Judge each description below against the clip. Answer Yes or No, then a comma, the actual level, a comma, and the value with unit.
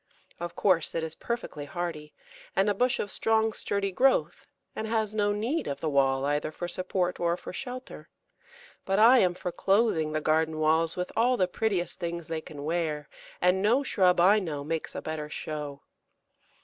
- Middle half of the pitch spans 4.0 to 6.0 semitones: Yes, average, 5.0 semitones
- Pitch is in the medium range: Yes, medium, 175 Hz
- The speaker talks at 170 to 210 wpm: Yes, average, 185 wpm